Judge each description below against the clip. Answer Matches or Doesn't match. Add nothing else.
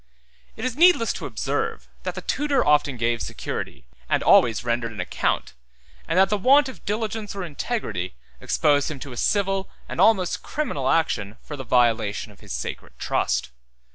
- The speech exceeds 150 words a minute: Matches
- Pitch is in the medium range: Matches